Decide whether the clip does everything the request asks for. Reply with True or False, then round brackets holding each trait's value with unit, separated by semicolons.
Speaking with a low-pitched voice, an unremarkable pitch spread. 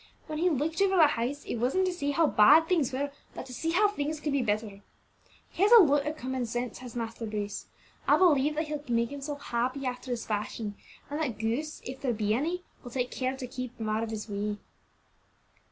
False (260 Hz; 4.7 semitones)